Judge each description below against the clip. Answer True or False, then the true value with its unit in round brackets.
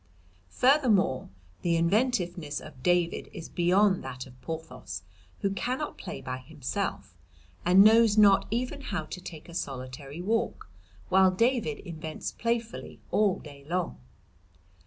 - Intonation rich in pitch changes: True (5.9 semitones)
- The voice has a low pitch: False (180 Hz)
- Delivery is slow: True (130 wpm)